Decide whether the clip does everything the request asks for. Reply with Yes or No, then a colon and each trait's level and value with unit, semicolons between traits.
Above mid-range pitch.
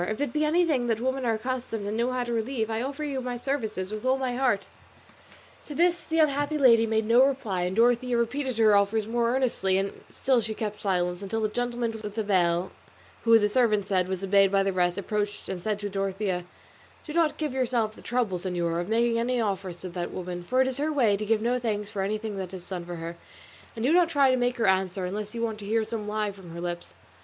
Yes: high, 220 Hz